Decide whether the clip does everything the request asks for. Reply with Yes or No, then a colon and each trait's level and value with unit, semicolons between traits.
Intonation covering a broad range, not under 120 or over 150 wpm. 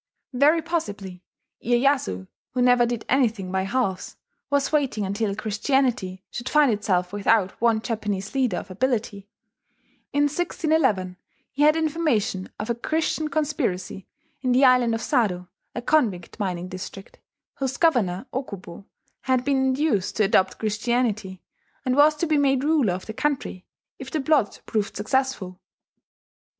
Yes: wide, 5.9 semitones; average, 140 wpm